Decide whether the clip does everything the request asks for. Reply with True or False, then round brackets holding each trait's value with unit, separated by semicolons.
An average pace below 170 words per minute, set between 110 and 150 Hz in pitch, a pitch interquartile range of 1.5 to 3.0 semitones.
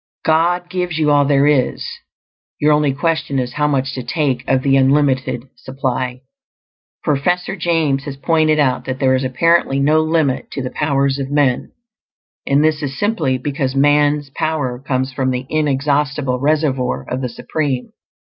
True (160 wpm; 140 Hz; 2.6 semitones)